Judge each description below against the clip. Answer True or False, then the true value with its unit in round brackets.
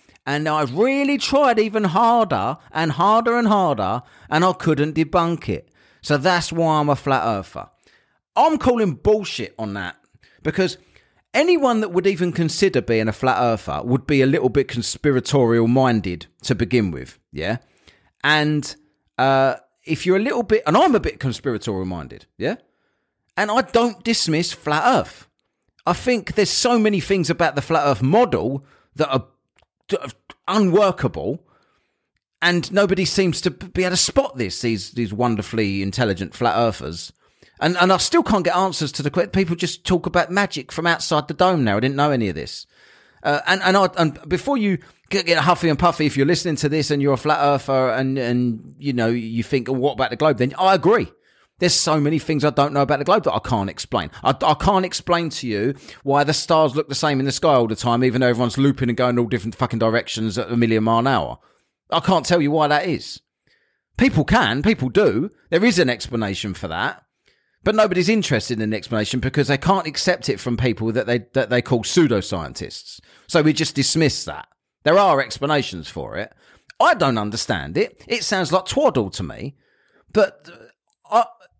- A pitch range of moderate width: False (6.7 semitones)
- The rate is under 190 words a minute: False (195 wpm)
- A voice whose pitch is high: False (150 Hz)